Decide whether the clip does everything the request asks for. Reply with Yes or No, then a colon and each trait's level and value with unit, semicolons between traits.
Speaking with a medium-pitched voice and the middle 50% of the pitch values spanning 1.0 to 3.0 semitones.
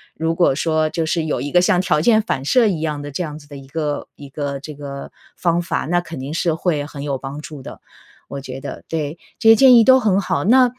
No: medium, 155 Hz; average, 3.7 semitones